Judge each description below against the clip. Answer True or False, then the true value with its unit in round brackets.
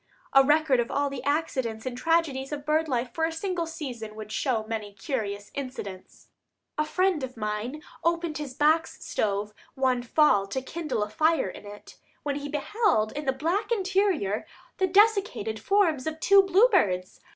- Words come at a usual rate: True (170 wpm)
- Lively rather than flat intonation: True (6.6 semitones)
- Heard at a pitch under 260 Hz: False (280 Hz)